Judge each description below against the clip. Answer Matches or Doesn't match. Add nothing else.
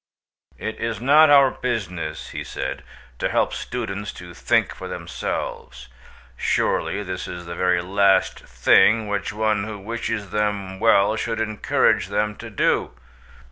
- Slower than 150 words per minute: Matches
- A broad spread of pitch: Doesn't match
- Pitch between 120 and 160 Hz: Doesn't match